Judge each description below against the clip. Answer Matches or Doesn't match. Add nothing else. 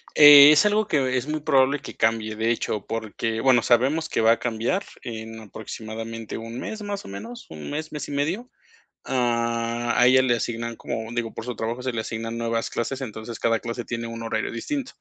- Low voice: Matches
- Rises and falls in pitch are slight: Doesn't match